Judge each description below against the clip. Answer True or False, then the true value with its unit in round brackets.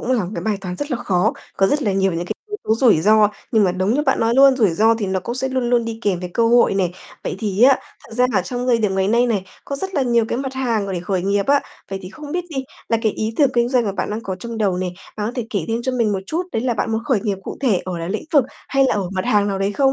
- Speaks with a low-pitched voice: False (220 Hz)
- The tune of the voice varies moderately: True (4.4 semitones)